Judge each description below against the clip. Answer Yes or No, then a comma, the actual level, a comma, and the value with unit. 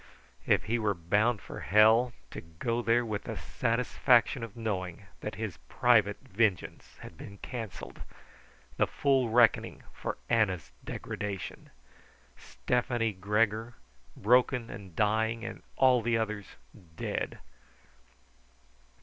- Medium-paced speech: No, slow, 115 wpm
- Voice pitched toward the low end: Yes, low, 110 Hz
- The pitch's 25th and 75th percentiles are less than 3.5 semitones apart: Yes, narrow, 2.6 semitones